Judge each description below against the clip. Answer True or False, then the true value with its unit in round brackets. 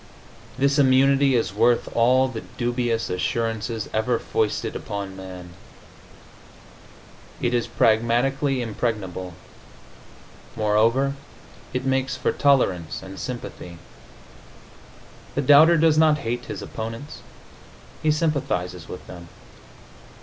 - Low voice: True (120 Hz)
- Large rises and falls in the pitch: False (4.4 semitones)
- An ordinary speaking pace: False (100 wpm)